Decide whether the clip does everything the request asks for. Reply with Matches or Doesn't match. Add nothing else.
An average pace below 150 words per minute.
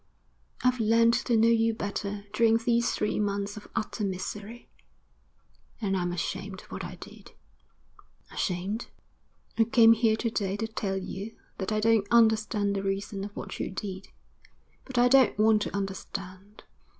Doesn't match